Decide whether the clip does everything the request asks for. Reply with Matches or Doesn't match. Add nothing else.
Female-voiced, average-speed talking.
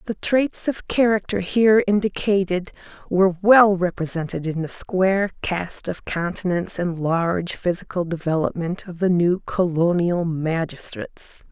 Doesn't match